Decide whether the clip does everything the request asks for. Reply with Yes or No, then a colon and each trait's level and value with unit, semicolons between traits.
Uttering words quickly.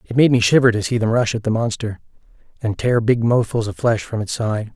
Yes: fast, 250 wpm